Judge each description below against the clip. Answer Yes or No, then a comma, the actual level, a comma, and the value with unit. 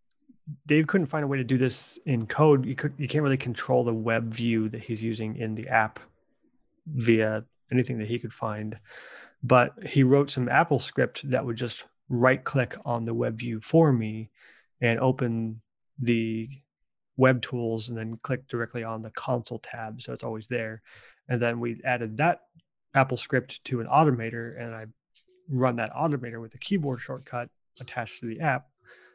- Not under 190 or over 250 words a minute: No, average, 180 wpm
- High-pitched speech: No, low, 120 Hz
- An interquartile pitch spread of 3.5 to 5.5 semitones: No, average, 3.1 semitones